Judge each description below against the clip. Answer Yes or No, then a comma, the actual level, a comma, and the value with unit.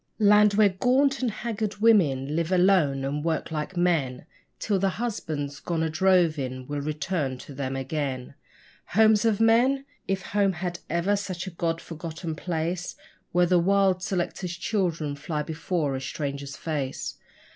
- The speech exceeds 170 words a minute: No, average, 155 wpm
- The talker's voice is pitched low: No, medium, 170 Hz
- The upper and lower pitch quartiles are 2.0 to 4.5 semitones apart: No, average, 5.0 semitones